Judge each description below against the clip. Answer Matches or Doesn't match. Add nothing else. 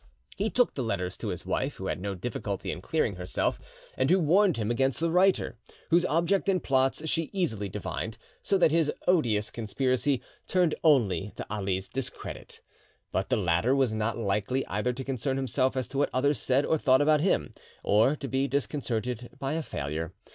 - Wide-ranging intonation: Matches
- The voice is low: Matches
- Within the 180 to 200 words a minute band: Matches